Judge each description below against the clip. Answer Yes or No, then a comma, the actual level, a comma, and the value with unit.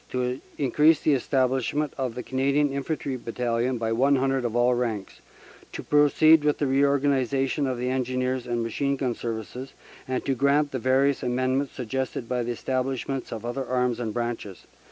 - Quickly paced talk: No, average, 160 wpm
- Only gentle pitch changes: Yes, narrow, 2.3 semitones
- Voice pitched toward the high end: No, low, 130 Hz